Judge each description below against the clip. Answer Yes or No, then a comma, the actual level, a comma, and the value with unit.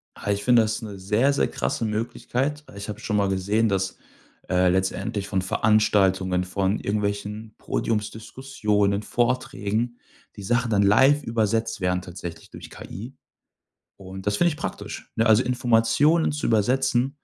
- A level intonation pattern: No, average, 3.3 semitones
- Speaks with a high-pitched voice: No, low, 105 Hz